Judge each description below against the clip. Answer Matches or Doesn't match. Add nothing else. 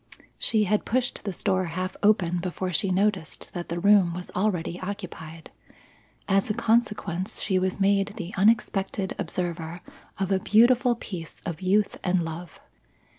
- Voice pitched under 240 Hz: Matches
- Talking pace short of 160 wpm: Matches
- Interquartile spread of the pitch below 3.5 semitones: Matches